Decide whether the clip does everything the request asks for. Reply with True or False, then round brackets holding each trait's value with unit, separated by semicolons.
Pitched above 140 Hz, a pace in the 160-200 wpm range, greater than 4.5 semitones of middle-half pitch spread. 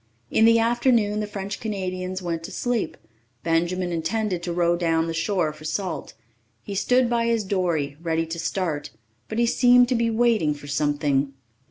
True (185 Hz; 175 wpm; 5.5 semitones)